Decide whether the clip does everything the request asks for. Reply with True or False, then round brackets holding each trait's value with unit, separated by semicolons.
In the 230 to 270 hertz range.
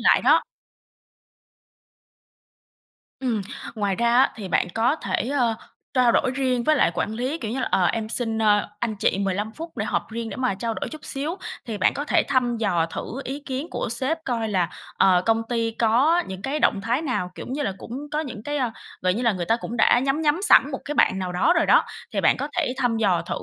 True (235 Hz)